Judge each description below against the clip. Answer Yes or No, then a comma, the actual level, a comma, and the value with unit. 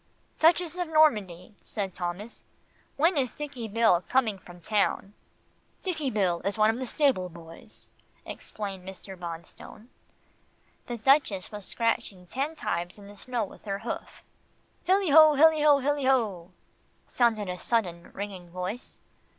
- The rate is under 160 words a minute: Yes, average, 140 wpm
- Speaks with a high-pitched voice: Yes, high, 215 Hz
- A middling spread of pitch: No, wide, 6.8 semitones